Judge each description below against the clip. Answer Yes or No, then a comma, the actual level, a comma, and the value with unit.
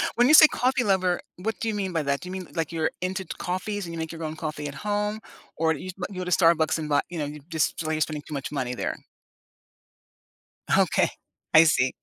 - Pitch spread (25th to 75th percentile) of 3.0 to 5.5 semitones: Yes, average, 3.6 semitones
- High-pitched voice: No, medium, 165 Hz